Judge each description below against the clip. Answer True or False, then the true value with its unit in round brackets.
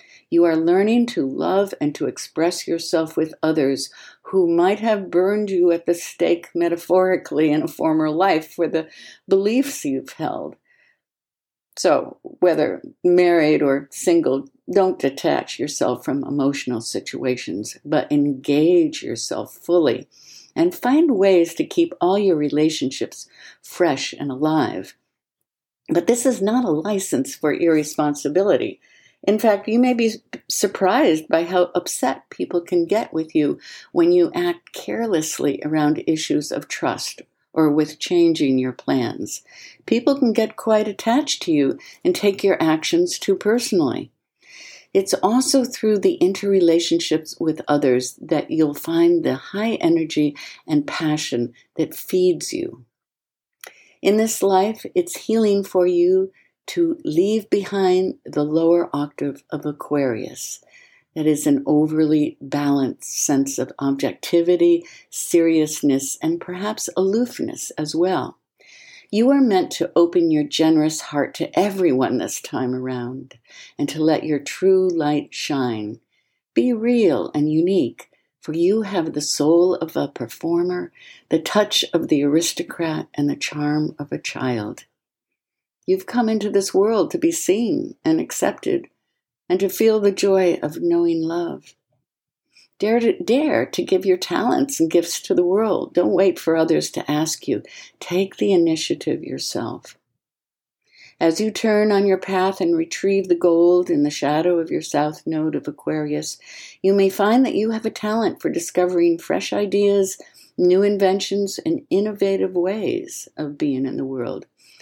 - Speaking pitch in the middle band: True (180 Hz)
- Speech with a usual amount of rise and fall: False (7.0 semitones)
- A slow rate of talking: False (145 wpm)